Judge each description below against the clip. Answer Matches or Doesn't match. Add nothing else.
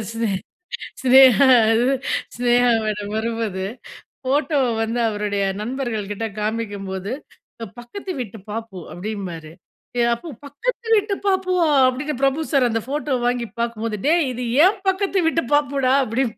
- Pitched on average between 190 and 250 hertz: Matches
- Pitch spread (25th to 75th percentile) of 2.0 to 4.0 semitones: Doesn't match